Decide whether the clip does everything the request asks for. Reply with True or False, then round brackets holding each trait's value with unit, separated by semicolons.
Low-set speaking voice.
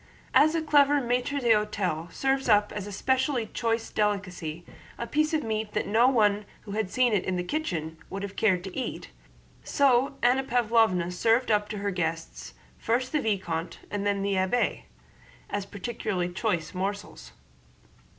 False (210 Hz)